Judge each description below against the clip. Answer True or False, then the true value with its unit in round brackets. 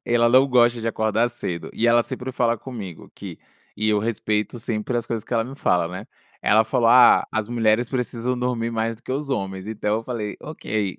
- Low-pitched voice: True (115 Hz)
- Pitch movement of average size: False (2.1 semitones)